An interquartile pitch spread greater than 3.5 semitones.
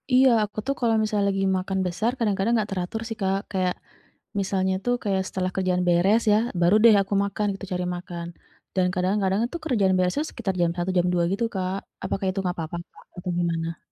No: narrow, 2.5 semitones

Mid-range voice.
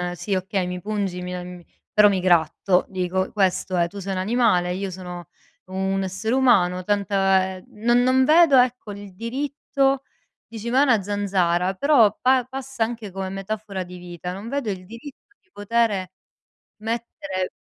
No: high, 200 Hz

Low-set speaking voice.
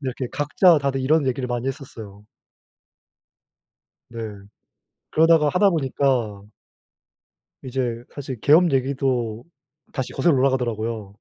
Yes: low, 130 Hz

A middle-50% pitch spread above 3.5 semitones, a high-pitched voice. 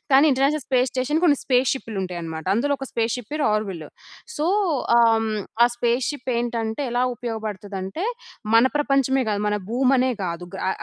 Yes: average, 4.0 semitones; high, 240 Hz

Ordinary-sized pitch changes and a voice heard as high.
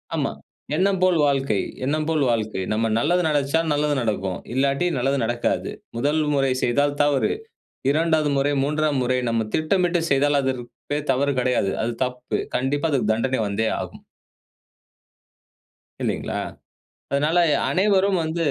No: average, 3.7 semitones; medium, 140 Hz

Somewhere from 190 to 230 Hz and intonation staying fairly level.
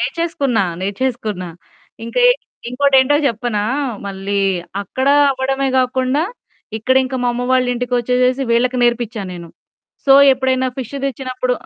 No: very high, 255 Hz; narrow, 2.0 semitones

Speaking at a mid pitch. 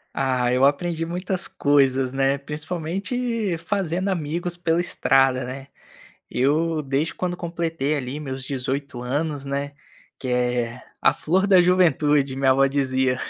Yes: medium, 145 Hz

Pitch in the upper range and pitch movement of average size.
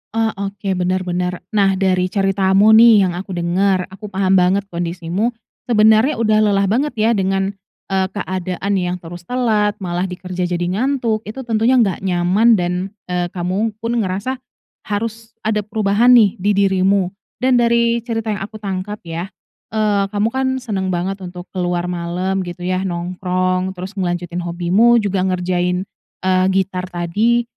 Yes: high, 195 Hz; average, 3.1 semitones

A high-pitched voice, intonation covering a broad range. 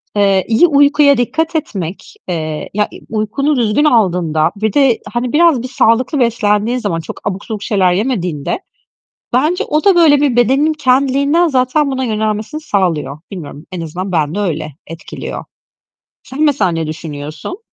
Yes: high, 220 Hz; wide, 7.6 semitones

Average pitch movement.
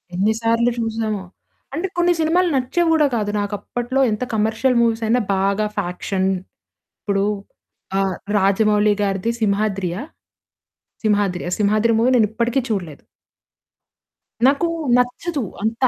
Yes: average, 3.5 semitones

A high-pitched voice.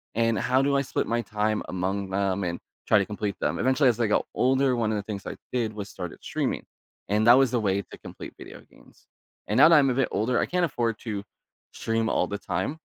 No: low, 110 Hz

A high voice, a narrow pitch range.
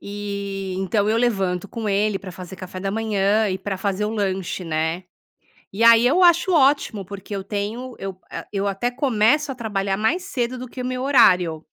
No: high, 205 Hz; average, 3.8 semitones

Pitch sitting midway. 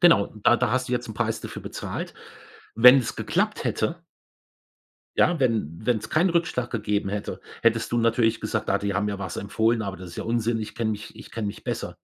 No: low, 115 Hz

